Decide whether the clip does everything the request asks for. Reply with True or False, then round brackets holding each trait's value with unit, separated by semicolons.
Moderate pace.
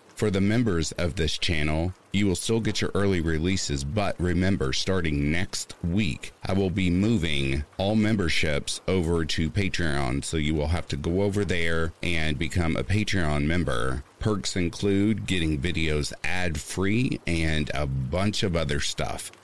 True (160 wpm)